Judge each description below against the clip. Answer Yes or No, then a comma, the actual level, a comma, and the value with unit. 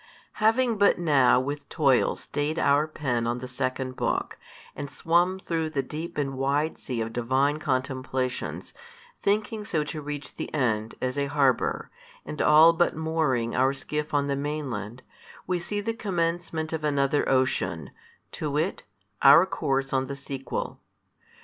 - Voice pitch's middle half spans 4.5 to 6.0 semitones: No, average, 3.6 semitones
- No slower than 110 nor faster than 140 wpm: No, average, 155 wpm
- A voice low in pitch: No, medium, 145 Hz